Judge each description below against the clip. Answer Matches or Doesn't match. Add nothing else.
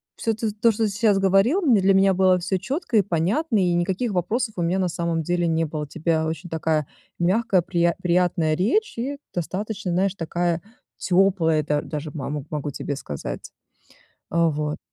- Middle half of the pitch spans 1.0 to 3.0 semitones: Doesn't match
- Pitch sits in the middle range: Matches